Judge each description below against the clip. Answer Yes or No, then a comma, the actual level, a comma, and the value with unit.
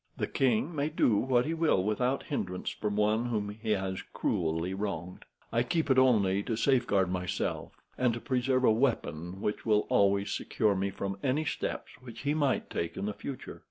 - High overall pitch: No, low, 110 Hz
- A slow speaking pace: No, average, 185 wpm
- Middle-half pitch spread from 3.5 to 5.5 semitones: Yes, average, 4.9 semitones